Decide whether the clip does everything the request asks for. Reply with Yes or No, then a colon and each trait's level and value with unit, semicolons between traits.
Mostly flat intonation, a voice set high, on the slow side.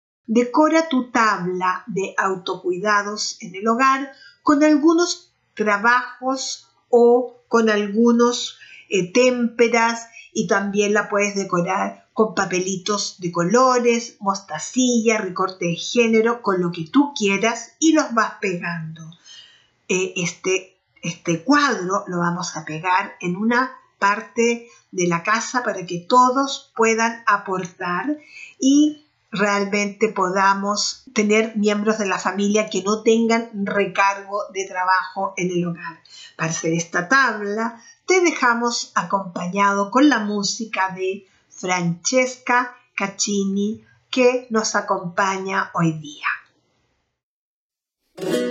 No: average, 4.1 semitones; high, 210 Hz; slow, 115 wpm